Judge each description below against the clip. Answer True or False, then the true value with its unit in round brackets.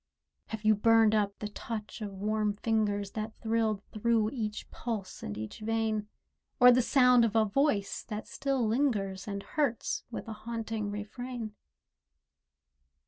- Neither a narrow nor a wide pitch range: False (1.9 semitones)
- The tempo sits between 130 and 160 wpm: True (145 wpm)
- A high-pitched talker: True (220 Hz)